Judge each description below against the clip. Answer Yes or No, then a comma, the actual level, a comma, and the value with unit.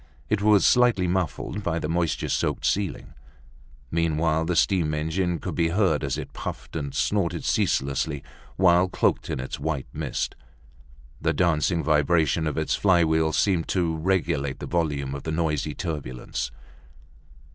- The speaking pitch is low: Yes, very low, 80 Hz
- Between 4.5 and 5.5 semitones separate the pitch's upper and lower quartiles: No, average, 2.9 semitones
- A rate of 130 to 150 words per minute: Yes, average, 145 wpm